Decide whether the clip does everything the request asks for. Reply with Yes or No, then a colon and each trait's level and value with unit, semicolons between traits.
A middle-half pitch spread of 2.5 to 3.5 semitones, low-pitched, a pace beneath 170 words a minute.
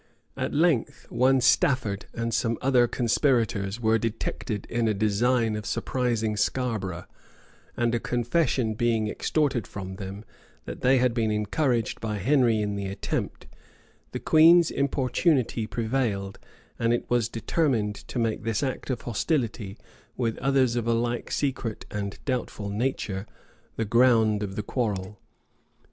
Yes: average, 3.1 semitones; low, 115 Hz; average, 140 wpm